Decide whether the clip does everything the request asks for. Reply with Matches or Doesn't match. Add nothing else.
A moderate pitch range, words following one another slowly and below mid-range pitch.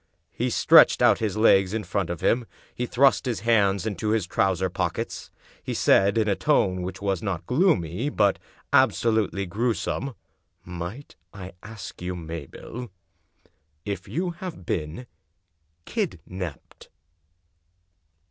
Matches